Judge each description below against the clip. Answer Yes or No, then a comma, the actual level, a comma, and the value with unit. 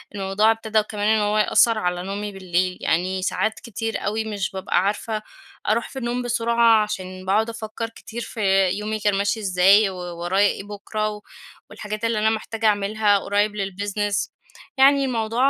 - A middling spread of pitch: No, narrow, 2.2 semitones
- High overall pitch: Yes, high, 210 Hz